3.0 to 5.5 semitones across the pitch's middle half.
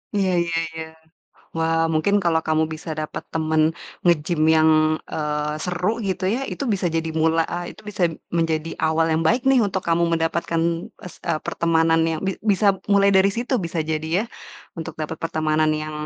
No: narrow, 2.6 semitones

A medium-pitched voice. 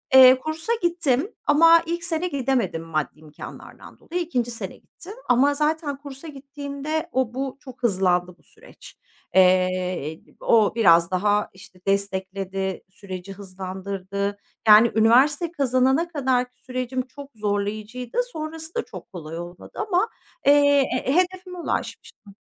No: very high, 250 Hz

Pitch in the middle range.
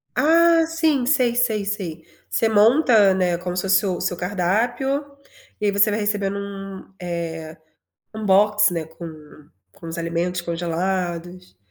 No: high, 195 Hz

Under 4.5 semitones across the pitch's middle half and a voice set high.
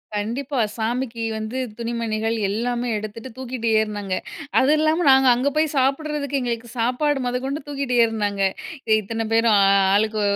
Yes: average, 3.4 semitones; high, 240 Hz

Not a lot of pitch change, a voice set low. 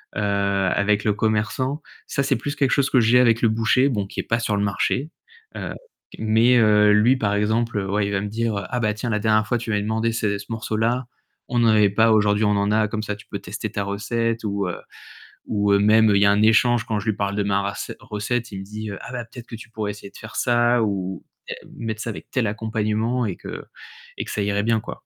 Yes: narrow, 2.1 semitones; low, 110 Hz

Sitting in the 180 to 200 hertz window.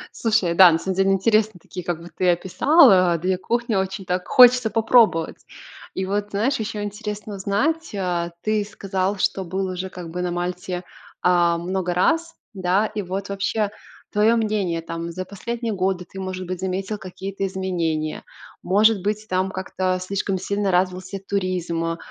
Yes: high, 190 Hz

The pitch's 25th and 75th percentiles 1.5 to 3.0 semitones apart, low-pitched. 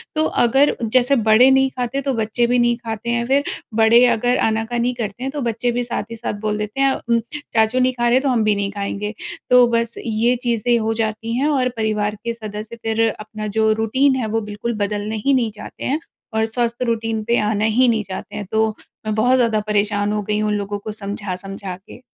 No: narrow, 2.4 semitones; high, 225 Hz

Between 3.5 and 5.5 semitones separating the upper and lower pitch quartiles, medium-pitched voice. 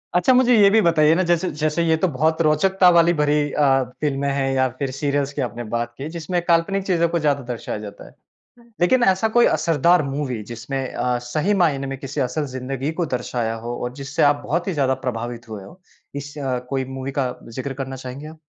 Yes: average, 4.4 semitones; medium, 145 Hz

